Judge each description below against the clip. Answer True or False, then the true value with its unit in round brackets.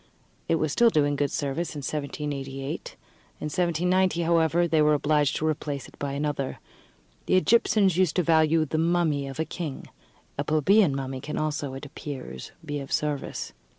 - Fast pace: False (170 wpm)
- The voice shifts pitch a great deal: False (2.9 semitones)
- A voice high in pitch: False (150 Hz)